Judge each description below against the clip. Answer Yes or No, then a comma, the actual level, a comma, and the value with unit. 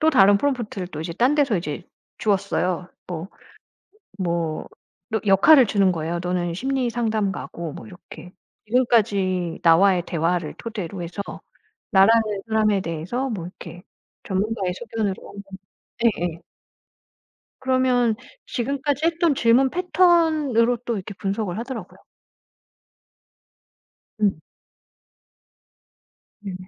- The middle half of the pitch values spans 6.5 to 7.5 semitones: No, average, 5.3 semitones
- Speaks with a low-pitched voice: No, high, 205 Hz